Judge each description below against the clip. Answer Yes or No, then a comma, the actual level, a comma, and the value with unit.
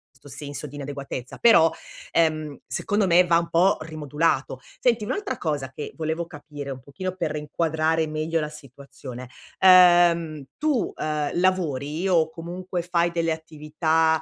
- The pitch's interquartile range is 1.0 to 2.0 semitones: No, average, 2.7 semitones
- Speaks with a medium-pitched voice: Yes, medium, 160 Hz